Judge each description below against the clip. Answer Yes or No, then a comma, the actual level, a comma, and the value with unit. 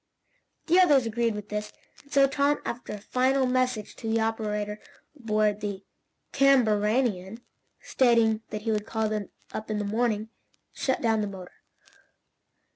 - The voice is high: Yes, high, 220 Hz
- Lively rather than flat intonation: No, average, 3.2 semitones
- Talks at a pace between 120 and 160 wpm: Yes, average, 150 wpm